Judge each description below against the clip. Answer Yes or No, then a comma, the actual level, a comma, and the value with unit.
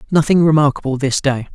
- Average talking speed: Yes, average, 155 wpm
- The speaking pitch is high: No, medium, 145 Hz